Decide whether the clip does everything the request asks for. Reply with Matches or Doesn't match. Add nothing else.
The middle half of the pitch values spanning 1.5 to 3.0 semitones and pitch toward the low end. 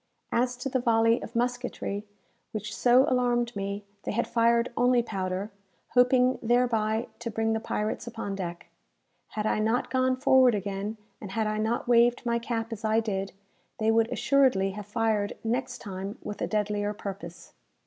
Doesn't match